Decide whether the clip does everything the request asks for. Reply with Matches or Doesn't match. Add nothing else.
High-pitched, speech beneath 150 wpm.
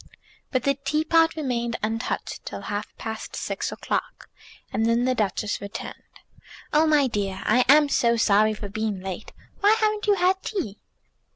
Doesn't match